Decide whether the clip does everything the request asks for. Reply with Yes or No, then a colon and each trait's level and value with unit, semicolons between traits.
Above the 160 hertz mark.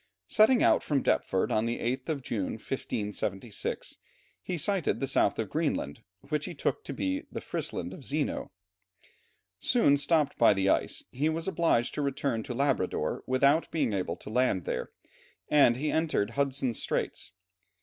No: low, 135 Hz